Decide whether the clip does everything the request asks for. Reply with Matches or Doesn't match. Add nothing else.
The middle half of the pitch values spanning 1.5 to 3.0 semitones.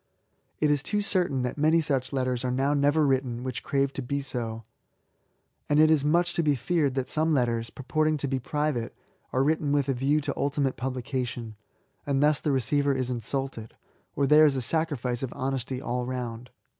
Matches